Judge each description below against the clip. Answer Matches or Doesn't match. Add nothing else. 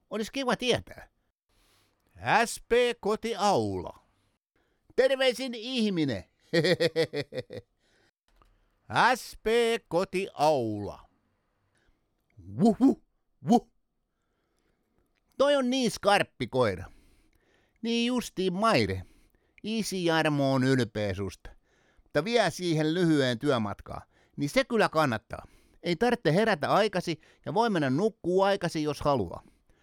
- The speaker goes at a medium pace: Doesn't match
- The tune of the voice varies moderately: Doesn't match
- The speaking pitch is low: Doesn't match